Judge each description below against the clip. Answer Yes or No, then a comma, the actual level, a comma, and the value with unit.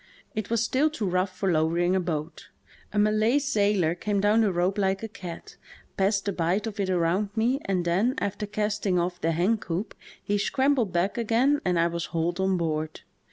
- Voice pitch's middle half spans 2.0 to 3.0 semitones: No, average, 3.5 semitones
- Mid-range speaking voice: No, high, 195 Hz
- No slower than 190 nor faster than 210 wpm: Yes, average, 200 wpm